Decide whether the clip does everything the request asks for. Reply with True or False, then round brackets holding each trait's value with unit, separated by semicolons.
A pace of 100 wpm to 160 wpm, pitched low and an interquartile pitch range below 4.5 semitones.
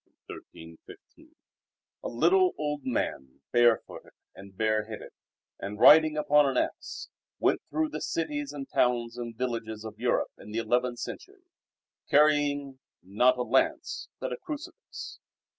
False (135 wpm; 125 Hz; 5.2 semitones)